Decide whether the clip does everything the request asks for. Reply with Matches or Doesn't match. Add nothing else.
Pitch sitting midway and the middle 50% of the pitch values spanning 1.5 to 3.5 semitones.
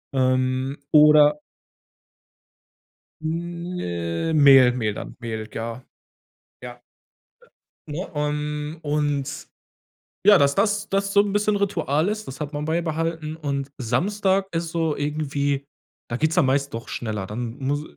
Doesn't match